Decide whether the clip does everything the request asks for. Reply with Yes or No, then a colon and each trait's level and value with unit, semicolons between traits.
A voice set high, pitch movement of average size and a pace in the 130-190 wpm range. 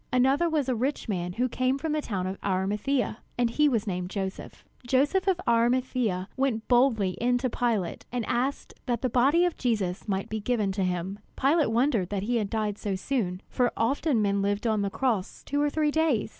No: high, 235 Hz; average, 4.8 semitones; average, 200 wpm